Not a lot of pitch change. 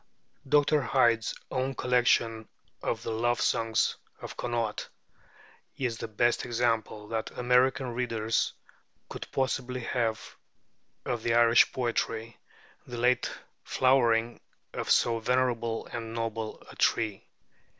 Yes: narrow, 1.7 semitones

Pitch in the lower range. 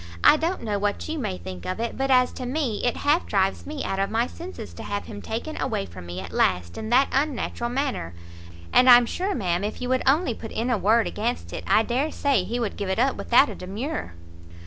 No: high, 235 Hz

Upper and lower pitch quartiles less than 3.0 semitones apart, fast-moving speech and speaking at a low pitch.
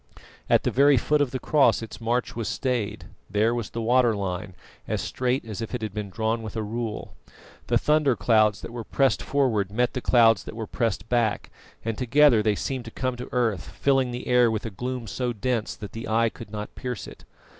Yes: narrow, 2.6 semitones; fast, 220 wpm; low, 115 Hz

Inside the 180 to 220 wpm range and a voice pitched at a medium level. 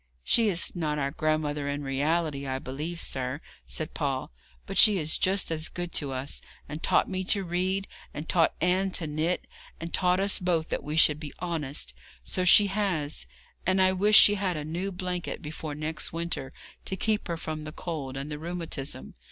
Yes: average, 195 wpm; medium, 160 Hz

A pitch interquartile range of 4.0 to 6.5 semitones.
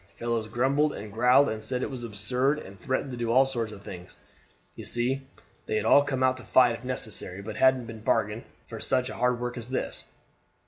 No: average, 3.1 semitones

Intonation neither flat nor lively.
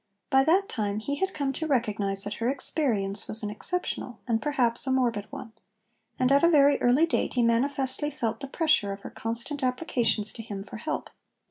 Yes: average, 4.5 semitones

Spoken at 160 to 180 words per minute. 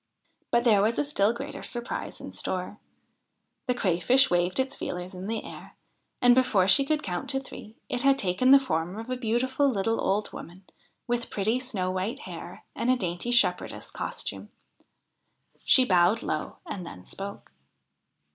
Yes: average, 165 wpm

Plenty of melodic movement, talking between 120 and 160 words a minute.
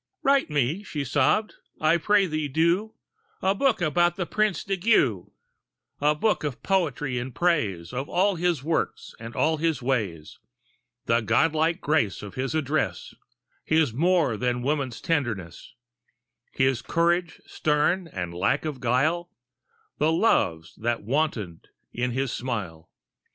Yes: wide, 6.1 semitones; average, 140 wpm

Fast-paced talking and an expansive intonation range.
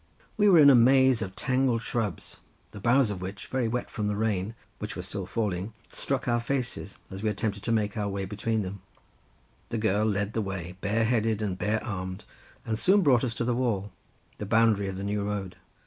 No: fast, 210 wpm; average, 3.0 semitones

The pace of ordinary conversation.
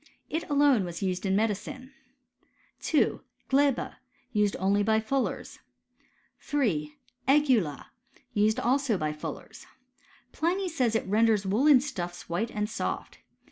No: slow, 130 wpm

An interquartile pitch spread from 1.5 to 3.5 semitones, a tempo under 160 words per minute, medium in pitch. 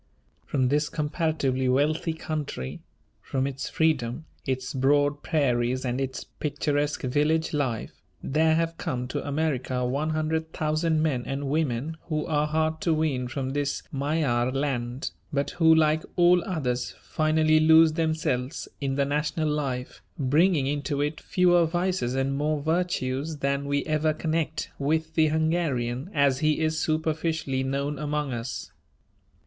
Yes: average, 2.9 semitones; average, 145 wpm; medium, 150 Hz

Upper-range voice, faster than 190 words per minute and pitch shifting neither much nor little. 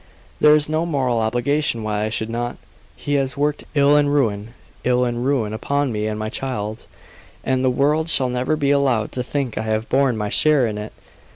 No: low, 125 Hz; fast, 205 wpm; average, 4.5 semitones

